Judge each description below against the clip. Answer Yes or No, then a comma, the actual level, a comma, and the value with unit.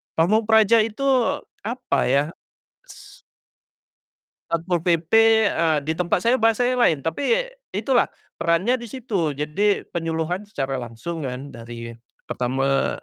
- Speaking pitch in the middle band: Yes, medium, 170 Hz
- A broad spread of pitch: Yes, wide, 7.7 semitones